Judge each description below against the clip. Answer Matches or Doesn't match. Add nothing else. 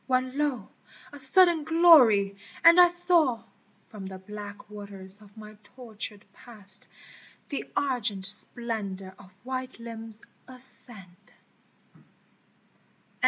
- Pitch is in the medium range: Doesn't match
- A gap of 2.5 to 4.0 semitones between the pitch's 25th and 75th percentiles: Doesn't match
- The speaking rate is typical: Doesn't match